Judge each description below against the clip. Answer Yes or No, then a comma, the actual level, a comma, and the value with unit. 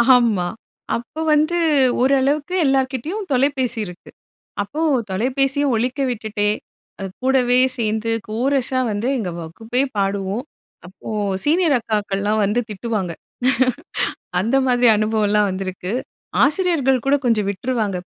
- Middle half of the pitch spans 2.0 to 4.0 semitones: No, average, 4.5 semitones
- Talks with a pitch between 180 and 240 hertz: Yes, high, 235 Hz